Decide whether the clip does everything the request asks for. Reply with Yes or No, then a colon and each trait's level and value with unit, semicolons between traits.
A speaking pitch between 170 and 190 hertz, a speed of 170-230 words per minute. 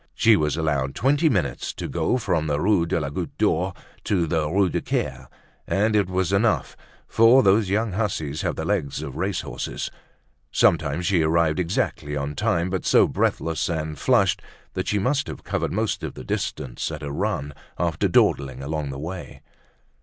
No: very low, 85 Hz; average, 180 wpm